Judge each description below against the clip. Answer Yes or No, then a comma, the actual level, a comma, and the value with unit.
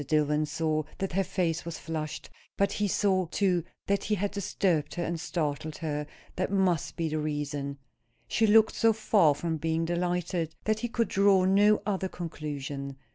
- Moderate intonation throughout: Yes, average, 4.3 semitones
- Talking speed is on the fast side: No, average, 175 wpm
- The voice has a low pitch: No, medium, 170 Hz